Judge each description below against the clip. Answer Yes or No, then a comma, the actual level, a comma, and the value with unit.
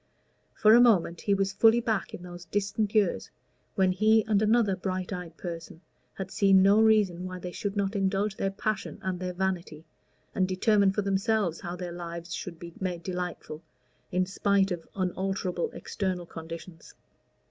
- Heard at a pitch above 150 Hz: Yes, high, 190 Hz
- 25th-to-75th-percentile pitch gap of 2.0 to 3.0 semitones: Yes, narrow, 2.4 semitones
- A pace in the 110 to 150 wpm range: No, average, 170 wpm